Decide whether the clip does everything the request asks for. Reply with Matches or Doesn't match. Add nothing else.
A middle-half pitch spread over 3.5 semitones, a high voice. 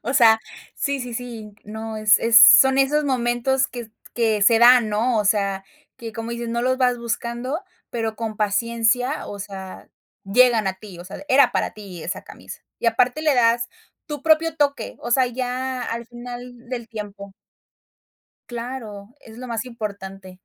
Doesn't match